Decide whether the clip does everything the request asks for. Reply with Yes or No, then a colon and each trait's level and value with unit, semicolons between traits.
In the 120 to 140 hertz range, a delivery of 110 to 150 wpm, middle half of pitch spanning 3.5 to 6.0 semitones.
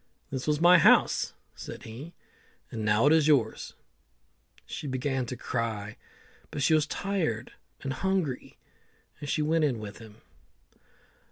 Yes: low, 135 Hz; average, 140 wpm; average, 5.2 semitones